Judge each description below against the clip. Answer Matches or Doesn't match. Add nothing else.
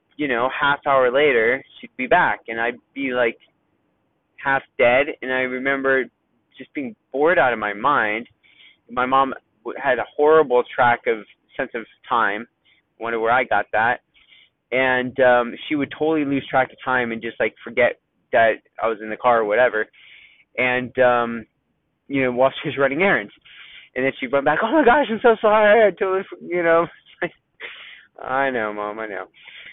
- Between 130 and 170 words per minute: Doesn't match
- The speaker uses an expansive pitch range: Doesn't match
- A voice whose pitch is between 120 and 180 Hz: Matches